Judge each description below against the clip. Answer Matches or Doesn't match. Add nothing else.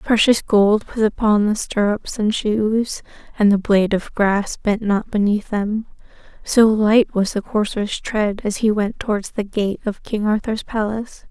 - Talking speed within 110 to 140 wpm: Doesn't match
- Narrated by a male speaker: Doesn't match